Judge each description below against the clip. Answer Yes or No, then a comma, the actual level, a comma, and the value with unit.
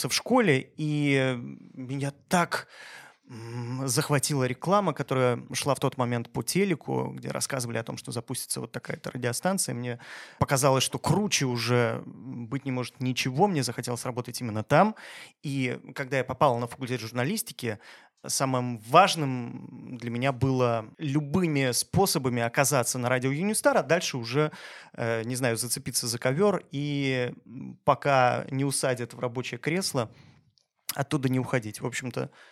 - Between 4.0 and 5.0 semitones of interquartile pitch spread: No, average, 2.9 semitones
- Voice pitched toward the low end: Yes, low, 130 Hz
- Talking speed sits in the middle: Yes, average, 140 wpm